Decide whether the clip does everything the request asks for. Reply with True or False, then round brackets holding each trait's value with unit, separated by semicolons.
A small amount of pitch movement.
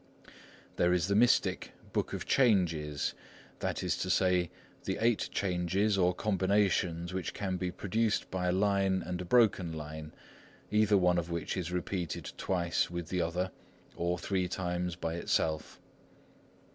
True (2.2 semitones)